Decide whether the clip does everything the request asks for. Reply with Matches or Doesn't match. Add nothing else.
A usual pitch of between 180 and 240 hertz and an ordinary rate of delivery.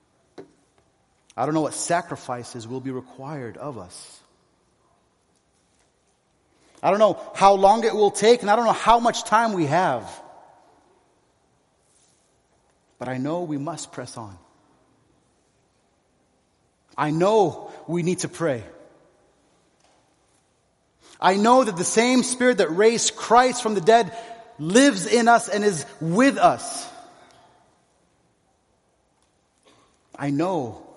Doesn't match